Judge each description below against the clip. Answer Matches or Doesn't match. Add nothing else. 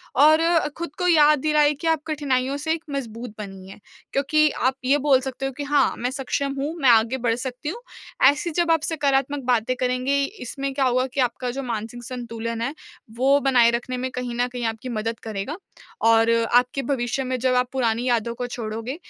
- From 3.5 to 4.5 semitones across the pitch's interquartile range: Doesn't match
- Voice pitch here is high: Matches